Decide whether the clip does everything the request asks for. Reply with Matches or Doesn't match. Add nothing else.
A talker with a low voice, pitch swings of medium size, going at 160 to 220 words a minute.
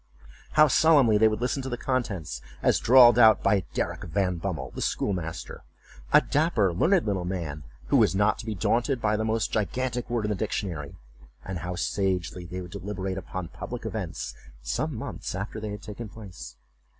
Matches